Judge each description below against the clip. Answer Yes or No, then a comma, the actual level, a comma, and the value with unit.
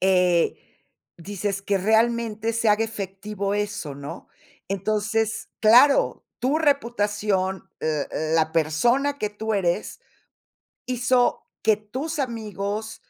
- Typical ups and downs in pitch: Yes, average, 3.1 semitones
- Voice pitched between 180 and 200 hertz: No, high, 210 Hz